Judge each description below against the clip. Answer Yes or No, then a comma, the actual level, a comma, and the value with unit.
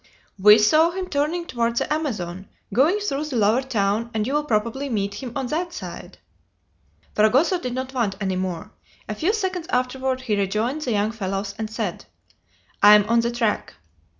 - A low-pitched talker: No, high, 235 Hz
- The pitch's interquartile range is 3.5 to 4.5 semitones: No, average, 5.2 semitones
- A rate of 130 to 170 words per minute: No, average, 180 wpm